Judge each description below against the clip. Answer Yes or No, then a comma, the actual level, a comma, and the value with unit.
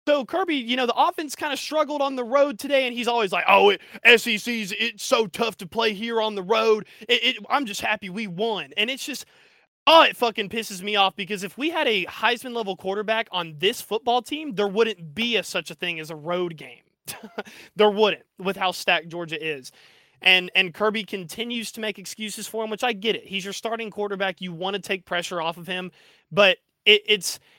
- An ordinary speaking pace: No, fast, 220 wpm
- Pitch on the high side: Yes, high, 215 Hz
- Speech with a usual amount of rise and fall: Yes, average, 3.8 semitones